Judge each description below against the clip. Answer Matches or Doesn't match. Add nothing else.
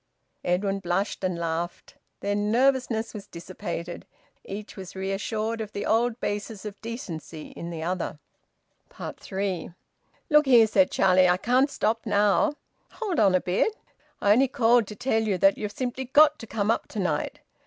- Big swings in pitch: Doesn't match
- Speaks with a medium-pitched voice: Doesn't match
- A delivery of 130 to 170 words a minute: Matches